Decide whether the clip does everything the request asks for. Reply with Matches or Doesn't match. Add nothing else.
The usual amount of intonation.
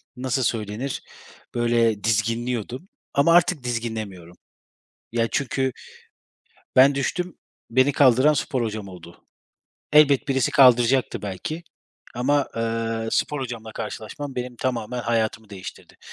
Matches